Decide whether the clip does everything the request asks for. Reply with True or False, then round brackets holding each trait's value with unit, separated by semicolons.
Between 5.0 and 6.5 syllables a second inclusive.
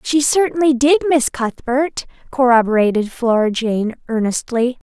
False (4.4 syllables/s)